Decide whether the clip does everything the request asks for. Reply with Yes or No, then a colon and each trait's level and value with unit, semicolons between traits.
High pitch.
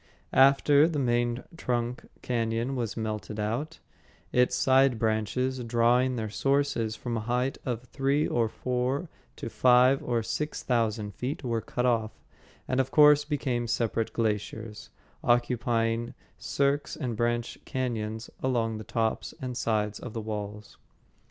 No: low, 120 Hz